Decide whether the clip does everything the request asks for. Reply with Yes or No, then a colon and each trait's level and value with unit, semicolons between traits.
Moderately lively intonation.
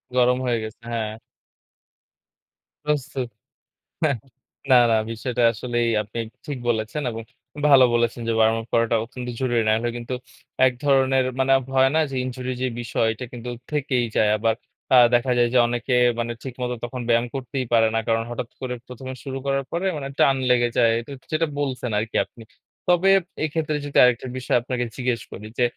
No: narrow, 2.3 semitones